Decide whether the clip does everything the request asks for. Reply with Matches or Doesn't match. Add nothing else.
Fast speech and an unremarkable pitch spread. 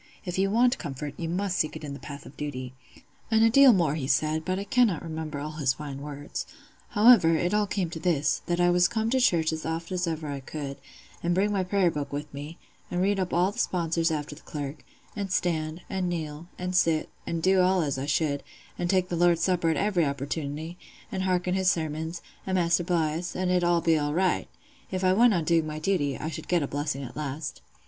Matches